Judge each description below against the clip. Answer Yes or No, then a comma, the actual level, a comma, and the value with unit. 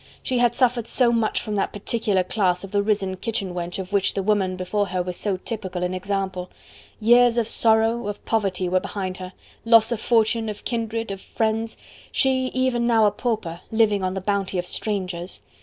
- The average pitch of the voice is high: Yes, high, 205 Hz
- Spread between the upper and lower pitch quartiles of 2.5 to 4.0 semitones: Yes, average, 3.5 semitones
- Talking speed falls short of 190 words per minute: No, average, 195 wpm